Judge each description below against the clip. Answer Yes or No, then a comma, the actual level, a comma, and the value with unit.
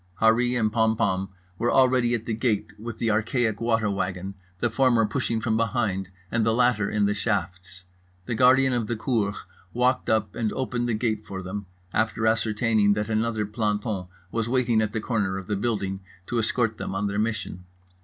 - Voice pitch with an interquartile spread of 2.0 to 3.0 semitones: Yes, narrow, 2.4 semitones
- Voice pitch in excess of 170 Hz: No, low, 110 Hz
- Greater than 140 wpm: Yes, average, 185 wpm